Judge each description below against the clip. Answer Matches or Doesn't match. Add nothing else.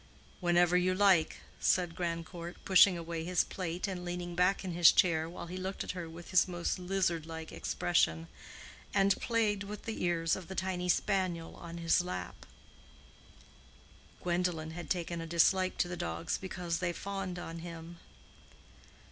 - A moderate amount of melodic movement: Doesn't match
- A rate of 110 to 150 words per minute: Doesn't match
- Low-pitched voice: Doesn't match